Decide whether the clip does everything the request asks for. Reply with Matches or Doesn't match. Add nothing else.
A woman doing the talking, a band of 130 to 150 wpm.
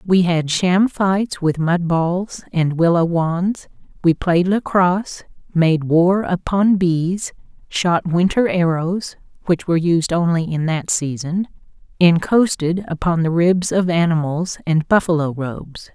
Matches